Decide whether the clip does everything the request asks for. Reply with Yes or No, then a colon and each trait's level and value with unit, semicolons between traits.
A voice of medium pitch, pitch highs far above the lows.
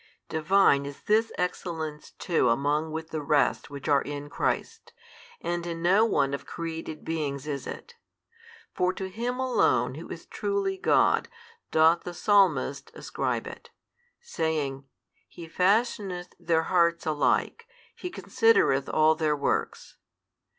No: medium, 165 Hz; average, 4.4 semitones